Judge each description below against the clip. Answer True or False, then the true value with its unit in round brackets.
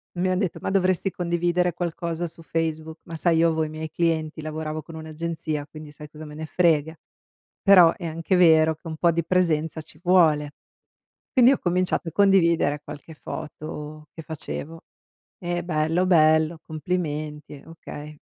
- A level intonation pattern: True (2.0 semitones)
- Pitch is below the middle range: False (160 Hz)